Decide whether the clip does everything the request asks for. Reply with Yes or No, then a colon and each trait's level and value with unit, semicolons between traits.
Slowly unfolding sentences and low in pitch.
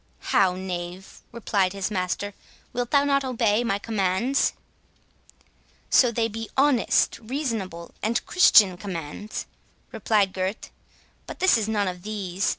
No: slow, 130 wpm; high, 210 Hz